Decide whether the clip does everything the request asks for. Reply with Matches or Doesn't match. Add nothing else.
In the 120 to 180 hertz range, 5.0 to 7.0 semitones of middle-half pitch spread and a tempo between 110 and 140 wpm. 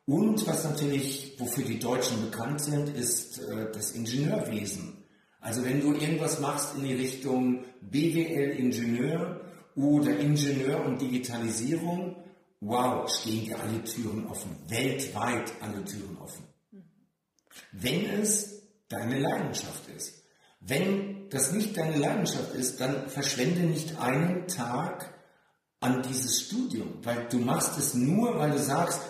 Matches